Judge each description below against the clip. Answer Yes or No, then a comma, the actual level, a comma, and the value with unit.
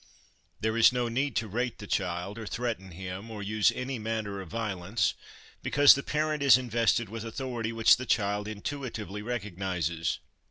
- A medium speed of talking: Yes, average, 165 wpm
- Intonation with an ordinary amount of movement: Yes, average, 3.5 semitones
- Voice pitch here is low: Yes, low, 110 Hz